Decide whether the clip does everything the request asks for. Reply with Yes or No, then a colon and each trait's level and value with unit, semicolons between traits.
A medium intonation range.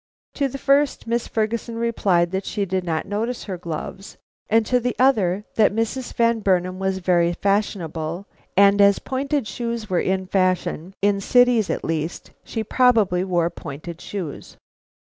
Yes: average, 4.4 semitones